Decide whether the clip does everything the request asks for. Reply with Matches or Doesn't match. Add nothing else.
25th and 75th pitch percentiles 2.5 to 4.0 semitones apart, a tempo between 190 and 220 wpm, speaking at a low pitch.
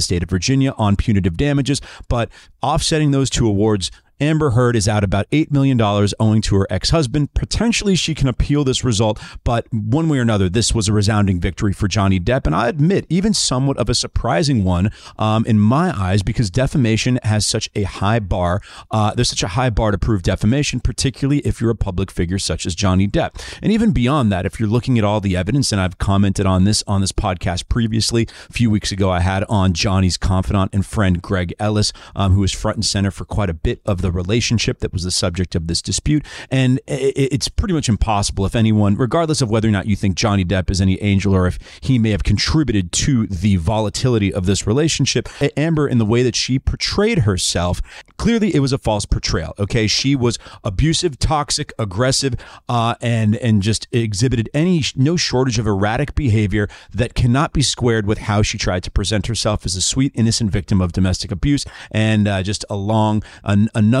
Doesn't match